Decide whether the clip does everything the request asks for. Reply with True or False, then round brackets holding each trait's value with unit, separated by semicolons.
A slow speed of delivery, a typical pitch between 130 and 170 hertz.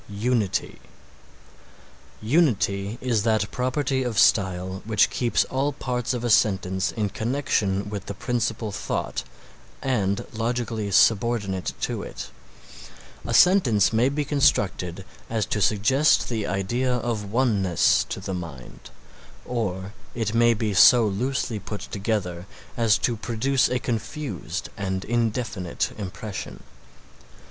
False (120 wpm; 110 Hz)